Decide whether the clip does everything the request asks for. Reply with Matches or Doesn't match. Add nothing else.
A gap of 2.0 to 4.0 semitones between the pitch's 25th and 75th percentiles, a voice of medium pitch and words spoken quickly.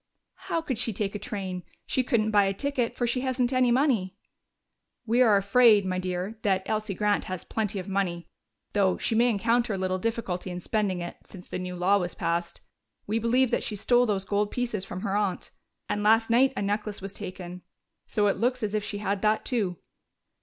Doesn't match